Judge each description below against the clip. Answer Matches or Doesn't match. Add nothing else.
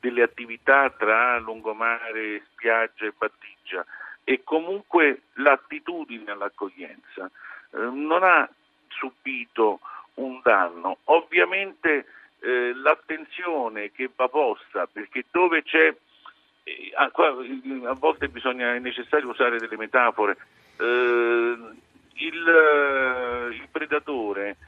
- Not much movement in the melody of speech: Doesn't match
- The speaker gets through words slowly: Matches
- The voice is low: Matches